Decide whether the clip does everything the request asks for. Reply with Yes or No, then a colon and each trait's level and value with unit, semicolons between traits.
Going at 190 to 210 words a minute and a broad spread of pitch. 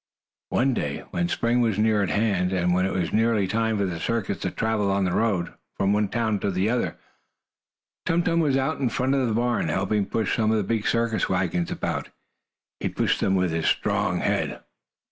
No: fast, 205 wpm; average, 3.6 semitones